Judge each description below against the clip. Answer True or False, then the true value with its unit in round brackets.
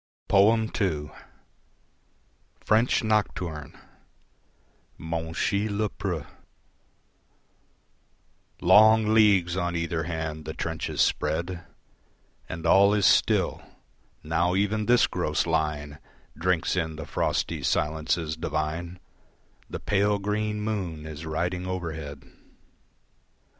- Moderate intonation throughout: True (4.5 semitones)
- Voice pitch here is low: True (85 Hz)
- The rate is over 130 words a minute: False (90 wpm)